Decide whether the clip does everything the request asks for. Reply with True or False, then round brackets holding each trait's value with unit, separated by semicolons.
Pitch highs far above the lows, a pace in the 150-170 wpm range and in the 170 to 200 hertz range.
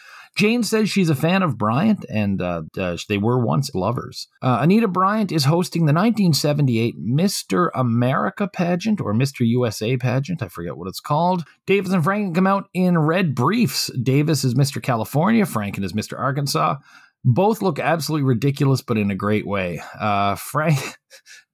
False (7.5 semitones; 165 wpm; 140 Hz)